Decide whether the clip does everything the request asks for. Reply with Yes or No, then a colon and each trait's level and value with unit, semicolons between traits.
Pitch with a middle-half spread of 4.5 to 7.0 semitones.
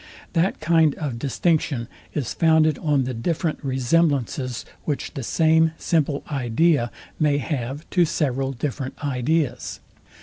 No: average, 3.6 semitones